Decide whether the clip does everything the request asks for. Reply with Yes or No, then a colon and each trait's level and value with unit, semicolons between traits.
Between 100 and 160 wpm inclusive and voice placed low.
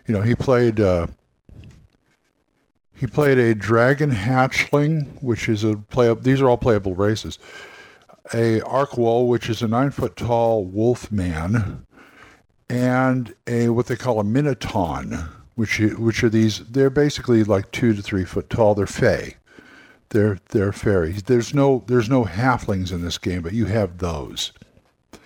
Yes: average, 155 wpm; low, 115 Hz